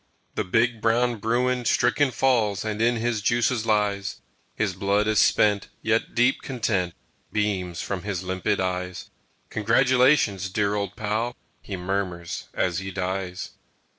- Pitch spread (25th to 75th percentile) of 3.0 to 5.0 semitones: Yes, average, 3.6 semitones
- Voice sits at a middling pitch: No, low, 105 Hz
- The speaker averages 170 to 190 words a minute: No, slow, 135 wpm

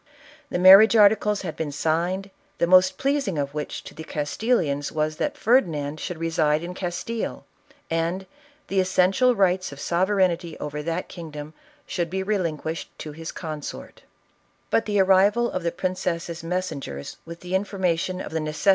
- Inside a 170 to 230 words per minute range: No, average, 160 wpm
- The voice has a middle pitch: Yes, medium, 175 Hz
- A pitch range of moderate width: Yes, average, 3.4 semitones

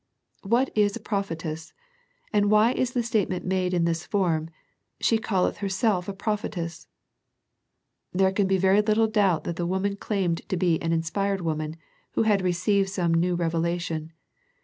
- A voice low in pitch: No, high, 190 Hz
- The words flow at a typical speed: Yes, average, 170 wpm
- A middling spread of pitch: Yes, average, 3.3 semitones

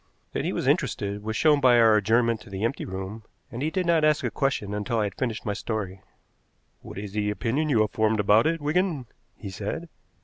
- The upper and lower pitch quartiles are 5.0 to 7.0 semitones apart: Yes, wide, 5.6 semitones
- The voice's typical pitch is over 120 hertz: No, low, 110 Hz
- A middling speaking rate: No, fast, 225 wpm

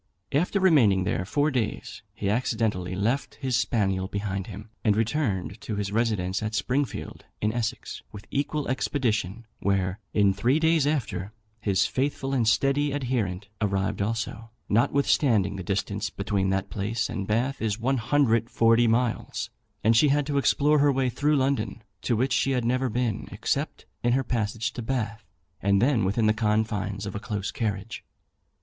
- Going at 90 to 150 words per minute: No, average, 160 wpm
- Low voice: Yes, low, 115 Hz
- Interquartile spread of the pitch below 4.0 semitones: No, average, 4.4 semitones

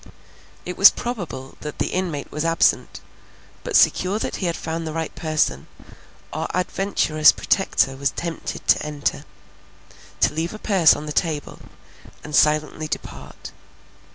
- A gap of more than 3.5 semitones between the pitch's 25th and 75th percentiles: No, average, 3.1 semitones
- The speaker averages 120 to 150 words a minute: Yes, average, 145 wpm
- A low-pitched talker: No, medium, 160 Hz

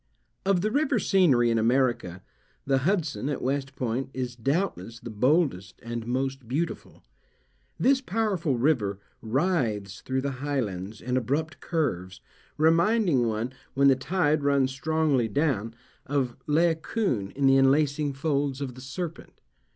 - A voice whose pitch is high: No, low, 135 Hz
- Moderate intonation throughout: Yes, average, 4.8 semitones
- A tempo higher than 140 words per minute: No, slow, 135 wpm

